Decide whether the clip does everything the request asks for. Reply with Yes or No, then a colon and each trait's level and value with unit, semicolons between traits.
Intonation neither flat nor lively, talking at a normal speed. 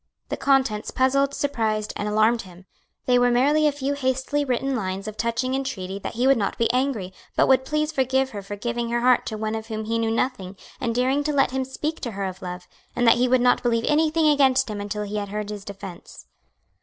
No: average, 4.1 semitones; fast, 230 wpm